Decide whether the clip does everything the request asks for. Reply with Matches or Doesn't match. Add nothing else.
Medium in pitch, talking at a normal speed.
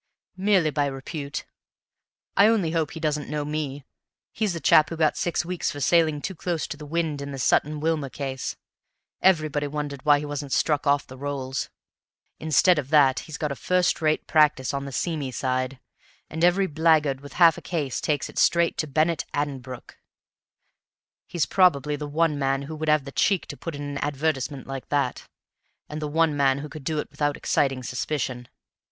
Matches